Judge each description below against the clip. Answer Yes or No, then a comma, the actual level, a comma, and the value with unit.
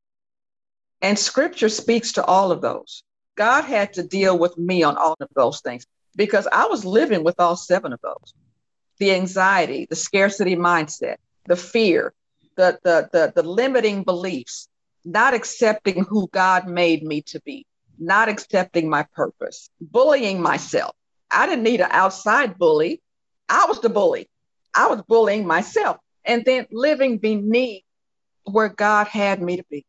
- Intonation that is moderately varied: Yes, average, 4.8 semitones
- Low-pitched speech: No, high, 195 Hz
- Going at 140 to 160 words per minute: Yes, average, 155 wpm